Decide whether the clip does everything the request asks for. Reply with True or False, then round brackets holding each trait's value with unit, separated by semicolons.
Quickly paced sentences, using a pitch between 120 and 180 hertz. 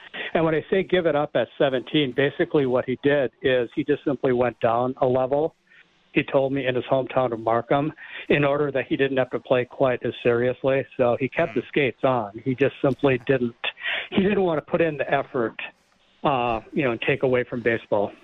True (215 wpm; 135 Hz)